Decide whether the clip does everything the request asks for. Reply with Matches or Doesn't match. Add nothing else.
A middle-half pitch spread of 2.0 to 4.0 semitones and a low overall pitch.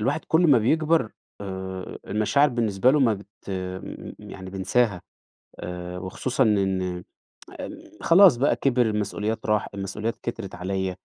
Doesn't match